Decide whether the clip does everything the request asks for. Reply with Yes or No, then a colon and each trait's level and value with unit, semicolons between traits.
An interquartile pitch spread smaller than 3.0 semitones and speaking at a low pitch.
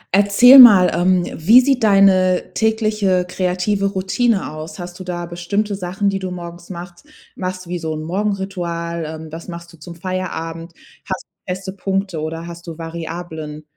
No: narrow, 2.6 semitones; medium, 180 Hz